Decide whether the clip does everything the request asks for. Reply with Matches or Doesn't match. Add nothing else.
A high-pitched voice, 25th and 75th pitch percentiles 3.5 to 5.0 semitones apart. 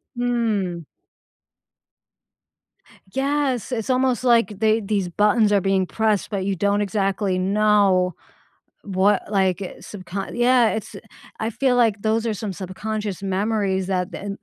Doesn't match